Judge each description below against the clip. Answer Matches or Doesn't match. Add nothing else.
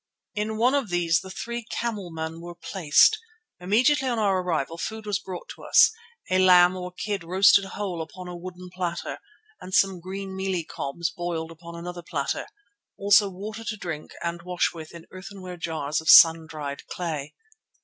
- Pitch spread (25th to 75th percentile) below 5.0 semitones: Matches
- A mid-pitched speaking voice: Matches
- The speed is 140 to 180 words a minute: Matches